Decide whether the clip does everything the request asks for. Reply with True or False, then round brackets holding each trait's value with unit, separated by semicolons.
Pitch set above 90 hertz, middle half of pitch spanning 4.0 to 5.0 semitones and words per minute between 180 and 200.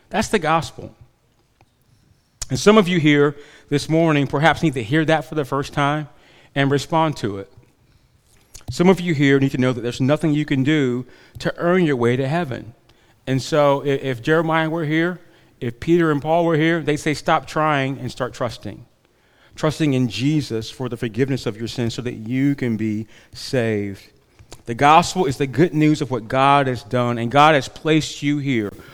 True (140 Hz; 4.4 semitones; 195 wpm)